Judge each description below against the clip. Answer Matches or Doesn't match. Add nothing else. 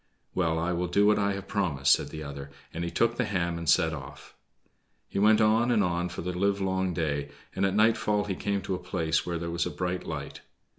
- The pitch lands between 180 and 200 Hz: Doesn't match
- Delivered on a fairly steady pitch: Doesn't match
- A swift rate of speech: Matches